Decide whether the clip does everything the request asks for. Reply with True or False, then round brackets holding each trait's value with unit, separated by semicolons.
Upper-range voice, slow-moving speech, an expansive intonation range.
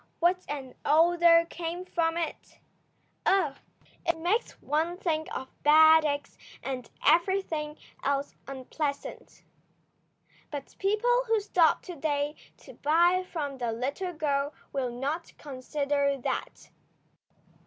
False (310 Hz; 115 wpm; 3.5 semitones)